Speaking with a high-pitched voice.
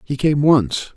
No: medium, 140 Hz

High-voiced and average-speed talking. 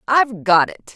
Yes: high, 225 Hz; average, 190 wpm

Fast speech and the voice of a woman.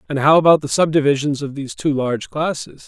No: fast, 210 wpm; male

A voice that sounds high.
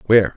No: low, 105 Hz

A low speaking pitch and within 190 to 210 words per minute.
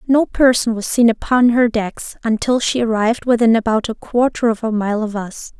No: high, 230 Hz; fast, 205 wpm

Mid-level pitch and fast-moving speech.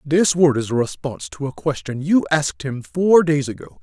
Yes: medium, 145 Hz; fast, 220 wpm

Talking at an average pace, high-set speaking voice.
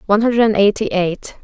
Yes: average, 165 wpm; high, 210 Hz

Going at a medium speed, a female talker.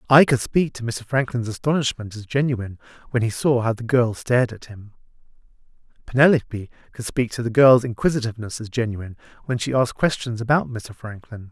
No: average, 175 wpm; male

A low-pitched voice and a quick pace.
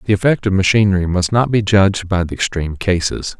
Yes: very low, 95 Hz; fast, 210 wpm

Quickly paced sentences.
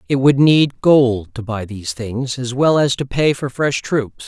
Yes: fast, 225 wpm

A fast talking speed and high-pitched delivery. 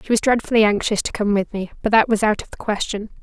Yes: fast, 280 wpm; high, 215 Hz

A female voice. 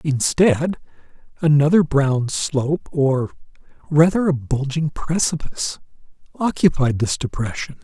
No: male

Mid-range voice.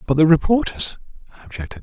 No: low, 125 Hz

